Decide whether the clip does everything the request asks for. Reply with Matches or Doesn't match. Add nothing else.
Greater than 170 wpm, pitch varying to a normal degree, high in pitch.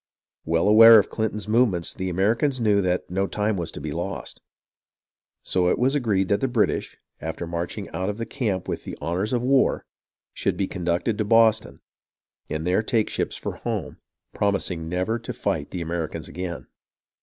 Doesn't match